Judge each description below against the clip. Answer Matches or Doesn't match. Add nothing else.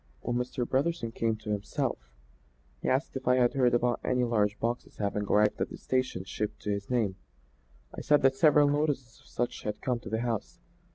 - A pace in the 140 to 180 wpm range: Doesn't match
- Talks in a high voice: Doesn't match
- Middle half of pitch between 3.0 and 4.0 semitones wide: Matches